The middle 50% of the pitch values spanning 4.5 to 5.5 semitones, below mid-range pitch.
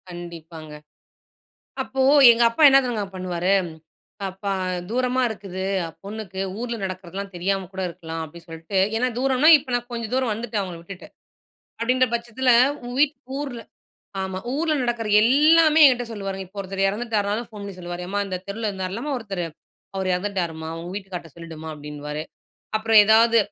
No: average, 4.8 semitones; high, 200 Hz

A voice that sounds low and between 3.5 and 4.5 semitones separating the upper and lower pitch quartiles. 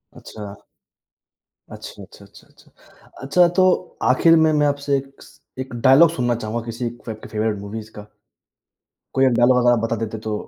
Yes: low, 120 Hz; average, 4.0 semitones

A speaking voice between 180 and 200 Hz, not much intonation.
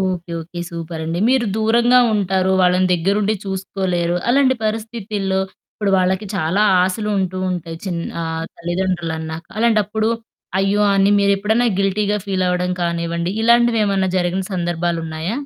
No: high, 190 Hz; average, 3.3 semitones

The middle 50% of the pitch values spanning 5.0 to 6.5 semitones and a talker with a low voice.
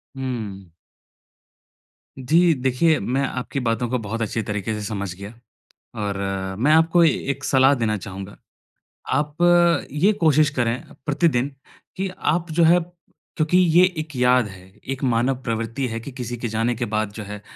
Yes: wide, 5.4 semitones; low, 125 Hz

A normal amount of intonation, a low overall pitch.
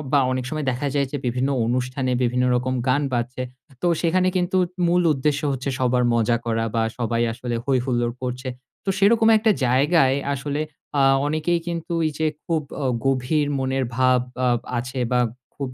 Yes: average, 3.4 semitones; low, 130 Hz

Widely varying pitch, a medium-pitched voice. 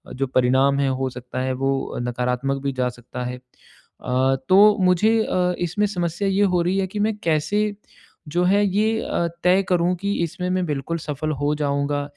Yes: wide, 6.0 semitones; medium, 160 Hz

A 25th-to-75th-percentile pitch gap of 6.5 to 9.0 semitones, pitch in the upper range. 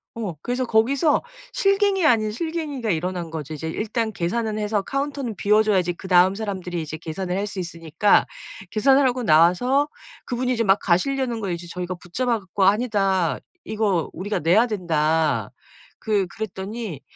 No: average, 5.3 semitones; high, 205 Hz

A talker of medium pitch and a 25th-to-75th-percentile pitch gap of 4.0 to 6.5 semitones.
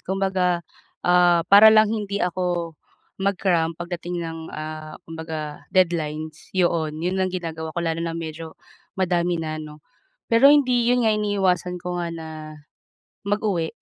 No: medium, 175 Hz; average, 2.9 semitones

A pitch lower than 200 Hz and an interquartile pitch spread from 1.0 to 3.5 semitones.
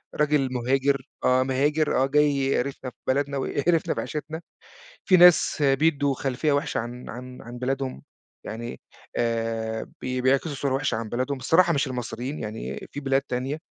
Yes: low, 135 Hz; narrow, 2.6 semitones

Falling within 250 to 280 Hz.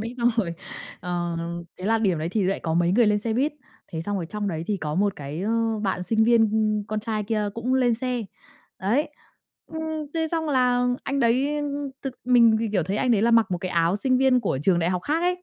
No: high, 220 Hz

